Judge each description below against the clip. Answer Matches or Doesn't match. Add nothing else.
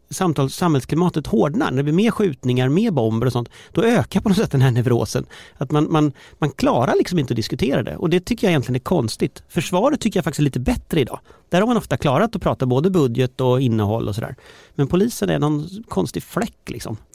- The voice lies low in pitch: Doesn't match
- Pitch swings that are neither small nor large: Doesn't match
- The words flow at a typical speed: Doesn't match